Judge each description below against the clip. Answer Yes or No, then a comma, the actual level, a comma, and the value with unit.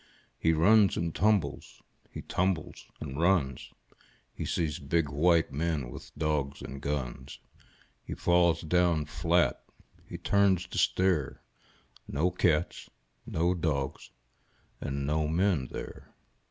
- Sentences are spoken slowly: Yes, slow, 125 wpm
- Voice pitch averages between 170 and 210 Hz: No, very low, 80 Hz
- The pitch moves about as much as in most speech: Yes, average, 3.6 semitones